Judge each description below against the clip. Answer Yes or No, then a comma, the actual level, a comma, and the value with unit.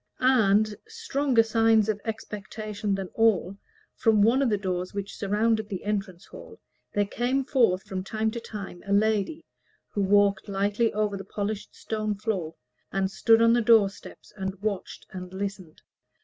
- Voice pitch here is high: Yes, high, 210 Hz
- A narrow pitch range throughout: Yes, narrow, 2.3 semitones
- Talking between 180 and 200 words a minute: No, average, 165 wpm